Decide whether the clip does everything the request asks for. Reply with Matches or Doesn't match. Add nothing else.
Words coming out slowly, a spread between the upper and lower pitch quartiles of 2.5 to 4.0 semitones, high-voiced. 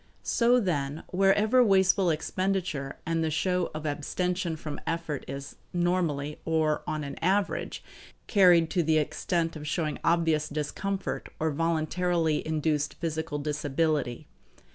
Doesn't match